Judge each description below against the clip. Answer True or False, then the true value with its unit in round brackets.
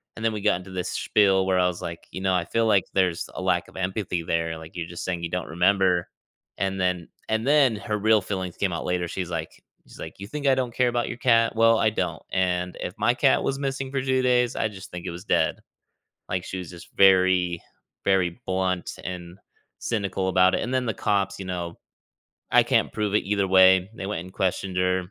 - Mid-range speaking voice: False (95 Hz)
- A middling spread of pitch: True (3.3 semitones)